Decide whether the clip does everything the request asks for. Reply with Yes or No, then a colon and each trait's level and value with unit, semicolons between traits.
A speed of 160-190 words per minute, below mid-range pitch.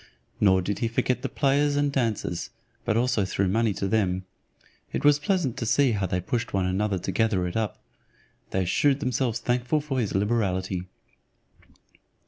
Yes: average, 170 wpm; low, 110 Hz